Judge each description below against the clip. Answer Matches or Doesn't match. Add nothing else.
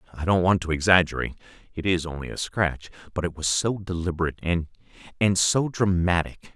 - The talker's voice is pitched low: Matches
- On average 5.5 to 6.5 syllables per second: Matches